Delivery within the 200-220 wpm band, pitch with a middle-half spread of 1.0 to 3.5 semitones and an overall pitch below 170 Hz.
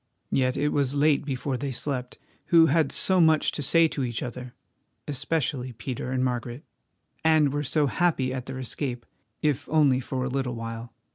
No: average, 165 wpm; average, 2.8 semitones; low, 135 Hz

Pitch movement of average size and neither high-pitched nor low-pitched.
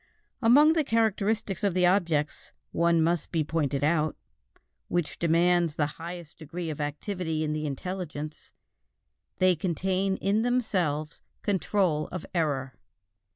Yes: average, 3.9 semitones; medium, 170 Hz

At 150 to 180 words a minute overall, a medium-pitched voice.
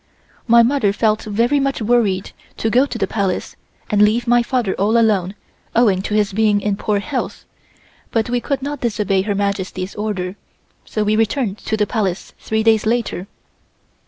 No: average, 175 wpm; high, 215 Hz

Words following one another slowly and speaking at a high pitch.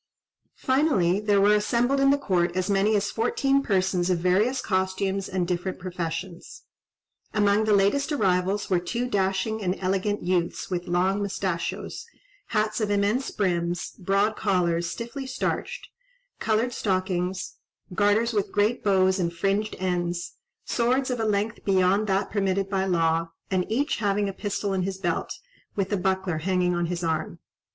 No: average, 155 wpm; high, 195 Hz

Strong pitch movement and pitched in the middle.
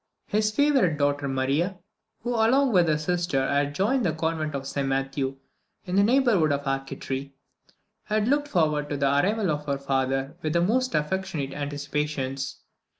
Yes: wide, 6.0 semitones; medium, 150 Hz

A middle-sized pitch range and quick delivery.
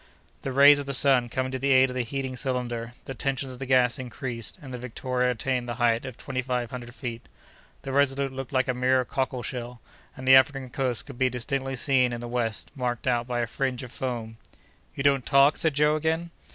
No: narrow, 1.9 semitones; fast, 225 wpm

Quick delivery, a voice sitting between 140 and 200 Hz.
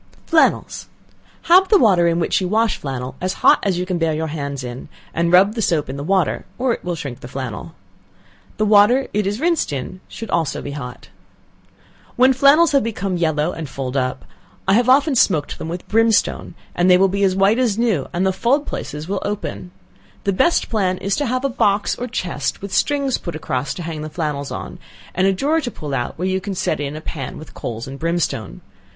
Yes: fast, 220 wpm; medium, 185 Hz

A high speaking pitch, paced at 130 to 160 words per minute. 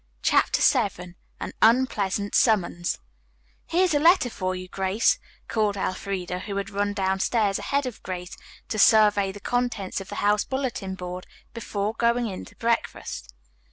Yes: high, 205 Hz; average, 150 wpm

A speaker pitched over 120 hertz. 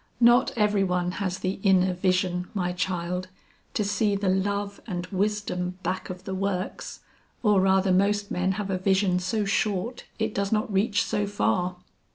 Yes: high, 190 Hz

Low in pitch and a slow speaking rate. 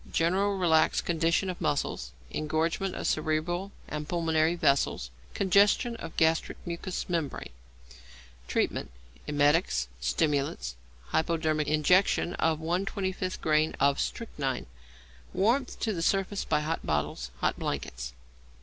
No: medium, 160 Hz; slow, 115 wpm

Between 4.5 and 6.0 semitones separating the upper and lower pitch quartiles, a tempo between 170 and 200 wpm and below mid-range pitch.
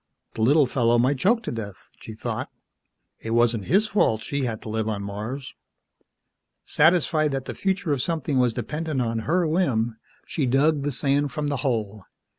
Yes: average, 5.1 semitones; average, 180 wpm; low, 130 Hz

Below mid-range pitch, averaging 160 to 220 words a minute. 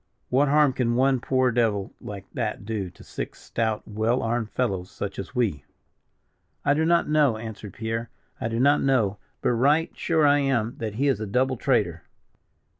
Yes: low, 120 Hz; average, 185 wpm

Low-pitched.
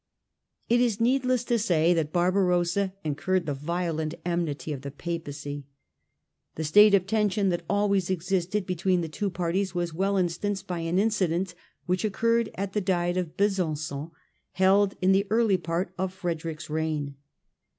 No: medium, 180 Hz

